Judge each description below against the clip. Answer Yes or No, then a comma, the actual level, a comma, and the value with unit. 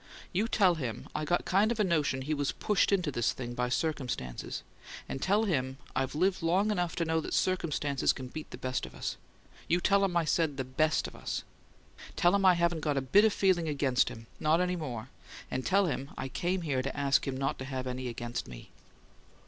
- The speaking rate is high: Yes, fast, 220 wpm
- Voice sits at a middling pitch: Yes, medium, 155 Hz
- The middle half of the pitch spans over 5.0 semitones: Yes, wide, 5.5 semitones